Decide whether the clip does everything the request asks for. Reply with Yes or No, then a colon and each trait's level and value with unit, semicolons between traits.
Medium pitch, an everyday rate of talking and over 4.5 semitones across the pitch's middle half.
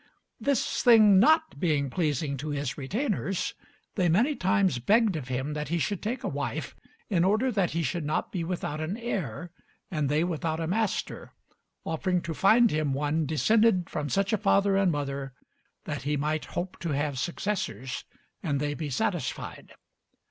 Yes: medium, 170 Hz; average, 170 wpm; average, 5.3 semitones